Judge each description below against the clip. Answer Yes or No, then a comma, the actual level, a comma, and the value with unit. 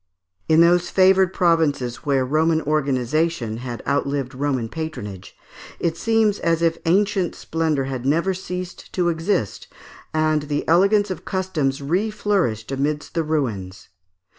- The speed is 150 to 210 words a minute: No, slow, 135 wpm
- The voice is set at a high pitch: No, medium, 155 Hz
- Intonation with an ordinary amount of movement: Yes, average, 4.7 semitones